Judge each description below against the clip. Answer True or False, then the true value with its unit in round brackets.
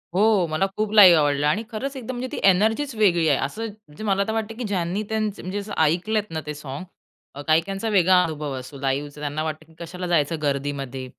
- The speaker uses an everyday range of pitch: False (6.1 semitones)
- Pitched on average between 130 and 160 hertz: False (175 Hz)